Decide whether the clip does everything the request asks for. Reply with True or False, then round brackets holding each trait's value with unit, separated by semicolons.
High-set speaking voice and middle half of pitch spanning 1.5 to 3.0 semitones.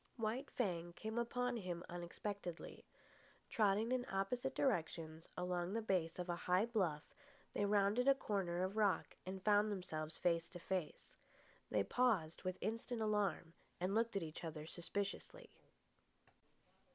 False (195 Hz; 4.1 semitones)